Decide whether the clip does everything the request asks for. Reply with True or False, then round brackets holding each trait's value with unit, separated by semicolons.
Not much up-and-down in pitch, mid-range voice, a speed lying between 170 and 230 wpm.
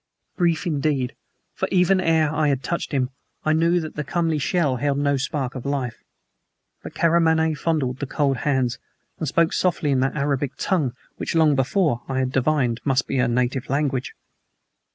False (3.5 semitones; 145 Hz; 175 wpm)